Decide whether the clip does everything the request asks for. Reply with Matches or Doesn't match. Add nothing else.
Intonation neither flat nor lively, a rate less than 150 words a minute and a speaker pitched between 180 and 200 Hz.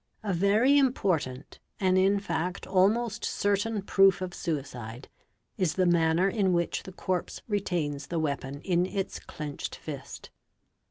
Matches